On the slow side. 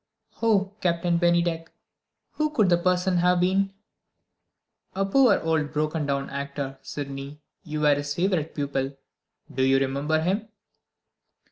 Yes: slow, 130 wpm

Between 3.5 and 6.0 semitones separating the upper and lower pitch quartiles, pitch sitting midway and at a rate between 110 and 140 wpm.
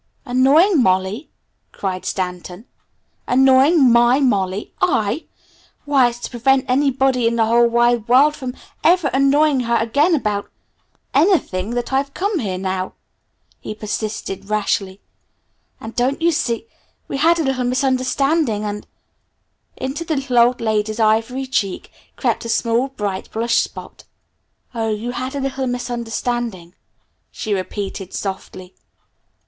No: average, 4.2 semitones; high, 240 Hz; slow, 135 wpm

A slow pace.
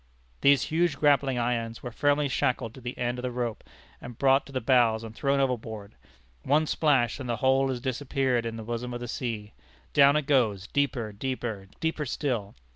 No: average, 195 wpm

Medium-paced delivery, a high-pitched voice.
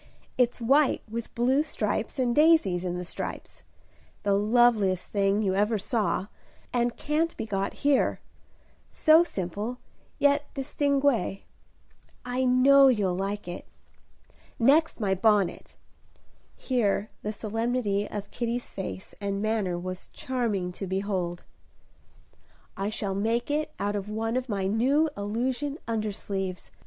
No: slow, 125 wpm; high, 220 Hz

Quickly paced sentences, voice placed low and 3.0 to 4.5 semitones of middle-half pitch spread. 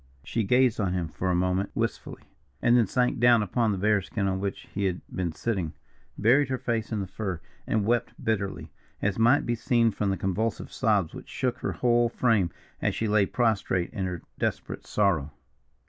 No: average, 195 wpm; low, 105 Hz; average, 3.8 semitones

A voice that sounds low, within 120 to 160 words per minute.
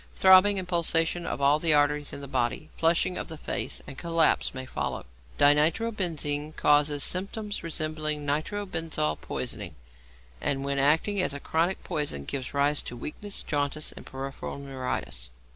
No: medium, 150 Hz; average, 150 wpm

